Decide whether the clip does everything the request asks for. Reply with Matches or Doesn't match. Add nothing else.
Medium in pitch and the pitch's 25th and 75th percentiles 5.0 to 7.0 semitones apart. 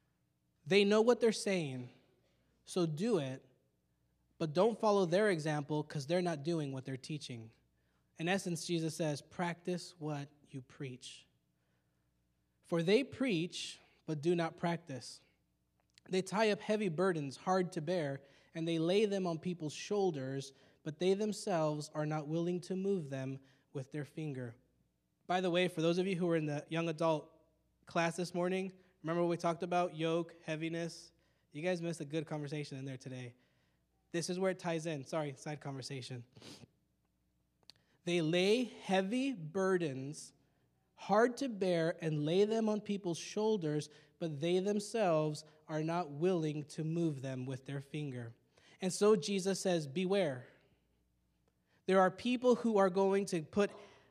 Matches